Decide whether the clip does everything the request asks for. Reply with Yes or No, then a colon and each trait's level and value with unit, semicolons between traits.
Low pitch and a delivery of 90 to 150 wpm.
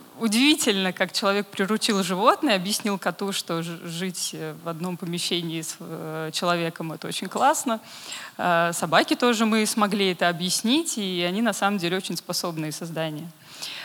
No: medium, 185 Hz; average, 135 wpm